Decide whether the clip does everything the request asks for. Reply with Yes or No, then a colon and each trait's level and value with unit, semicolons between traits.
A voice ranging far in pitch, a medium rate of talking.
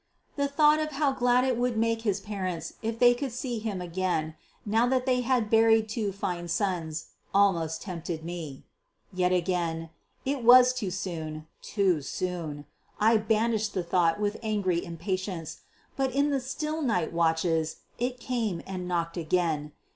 Yes: wide, 6.1 semitones; average, 160 wpm